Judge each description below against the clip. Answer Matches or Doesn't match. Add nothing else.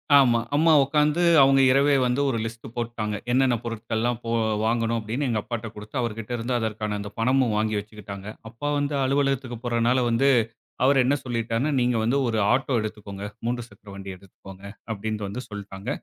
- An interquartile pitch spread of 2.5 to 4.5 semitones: Matches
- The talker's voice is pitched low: Matches